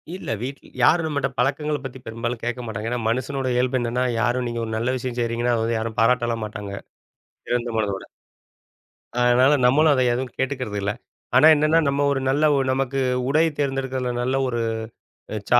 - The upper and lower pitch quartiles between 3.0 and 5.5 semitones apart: No, narrow, 2.4 semitones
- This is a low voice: Yes, low, 125 Hz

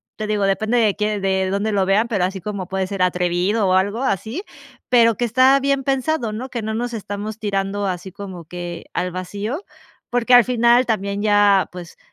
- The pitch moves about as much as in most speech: Yes, average, 3.5 semitones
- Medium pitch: No, high, 205 Hz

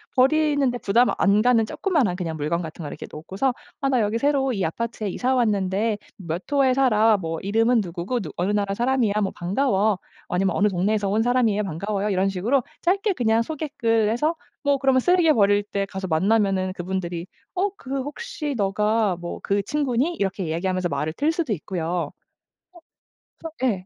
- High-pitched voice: Yes, high, 210 Hz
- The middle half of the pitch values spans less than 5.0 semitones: No, wide, 5.6 semitones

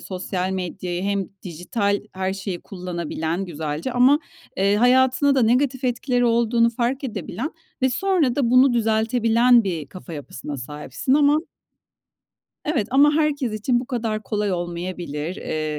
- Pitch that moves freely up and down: Yes, wide, 5.9 semitones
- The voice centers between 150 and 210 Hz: No, high, 220 Hz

